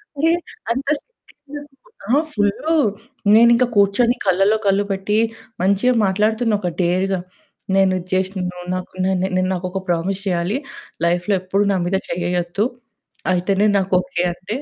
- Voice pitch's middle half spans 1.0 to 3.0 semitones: No, average, 3.6 semitones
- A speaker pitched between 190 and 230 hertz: Yes, high, 195 Hz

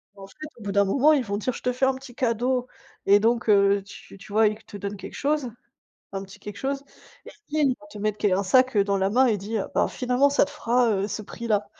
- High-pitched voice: Yes, high, 220 Hz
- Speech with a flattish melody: No, average, 4.0 semitones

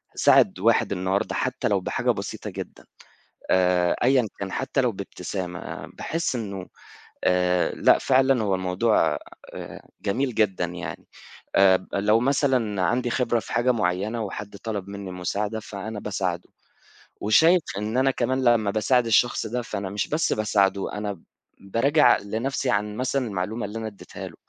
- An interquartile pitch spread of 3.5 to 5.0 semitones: Yes, average, 4.0 semitones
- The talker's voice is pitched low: Yes, low, 105 Hz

